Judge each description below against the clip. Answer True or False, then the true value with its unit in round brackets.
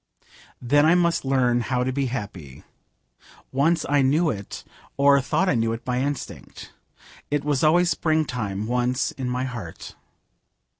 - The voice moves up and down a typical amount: True (3.2 semitones)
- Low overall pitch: True (130 Hz)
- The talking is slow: False (150 wpm)